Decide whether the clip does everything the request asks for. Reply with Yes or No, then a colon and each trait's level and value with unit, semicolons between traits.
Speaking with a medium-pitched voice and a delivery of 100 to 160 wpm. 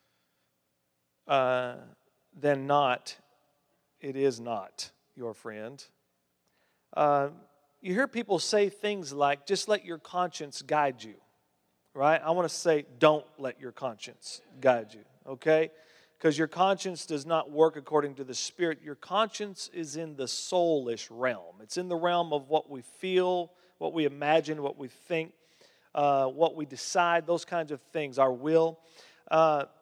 Yes: medium, 150 Hz; average, 150 wpm